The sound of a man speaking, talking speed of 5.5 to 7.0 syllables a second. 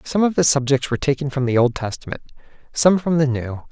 Yes: male; 6.1 syllables/s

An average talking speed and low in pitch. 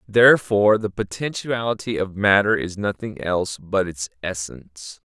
No: slow, 130 wpm; low, 100 Hz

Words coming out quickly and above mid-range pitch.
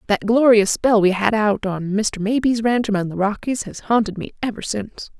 Yes: fast, 210 wpm; high, 215 Hz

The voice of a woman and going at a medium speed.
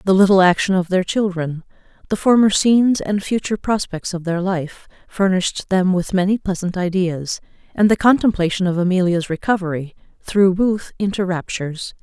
Yes: female; average, 155 wpm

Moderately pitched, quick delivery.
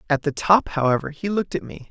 Yes: medium, 155 Hz; fast, 250 wpm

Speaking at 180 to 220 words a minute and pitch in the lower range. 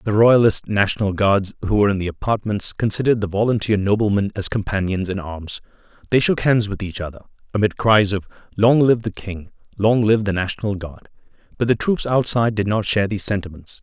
Yes: average, 190 wpm; low, 105 Hz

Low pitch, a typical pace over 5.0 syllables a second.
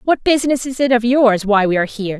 No: high, 235 Hz; 6.6 syllables/s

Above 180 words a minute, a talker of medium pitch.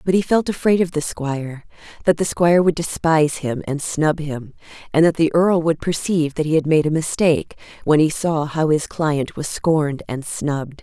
Yes: fast, 205 wpm; medium, 155 Hz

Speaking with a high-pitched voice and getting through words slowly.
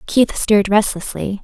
Yes: high, 205 Hz; slow, 125 wpm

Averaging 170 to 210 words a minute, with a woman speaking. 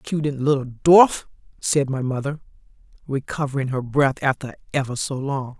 No: average, 140 wpm; female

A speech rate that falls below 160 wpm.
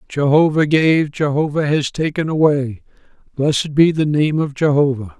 Yes: average, 140 wpm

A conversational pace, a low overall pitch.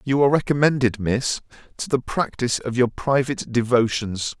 Yes: average, 150 wpm; low, 125 Hz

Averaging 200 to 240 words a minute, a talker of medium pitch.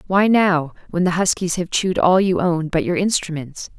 Yes: fast, 205 wpm; medium, 175 Hz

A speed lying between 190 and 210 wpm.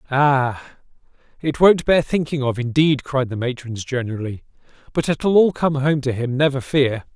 No: average, 170 wpm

